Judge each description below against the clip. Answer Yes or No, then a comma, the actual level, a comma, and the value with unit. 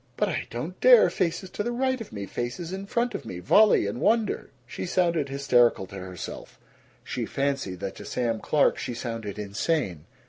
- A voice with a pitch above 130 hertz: Yes, medium, 140 Hz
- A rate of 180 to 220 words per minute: Yes, average, 195 wpm